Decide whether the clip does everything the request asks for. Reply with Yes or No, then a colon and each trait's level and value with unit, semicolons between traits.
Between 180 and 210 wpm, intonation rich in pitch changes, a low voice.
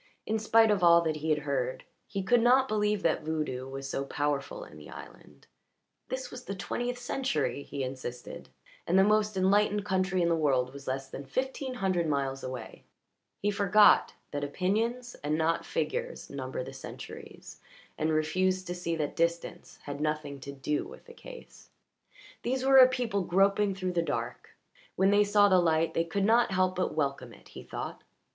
No: average, 185 wpm; wide, 6.2 semitones; medium, 185 Hz